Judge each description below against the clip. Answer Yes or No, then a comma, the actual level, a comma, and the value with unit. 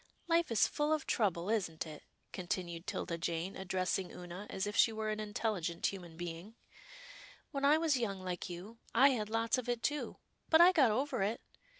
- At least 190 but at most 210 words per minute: Yes, average, 200 wpm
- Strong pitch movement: Yes, wide, 6.1 semitones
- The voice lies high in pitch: Yes, high, 210 Hz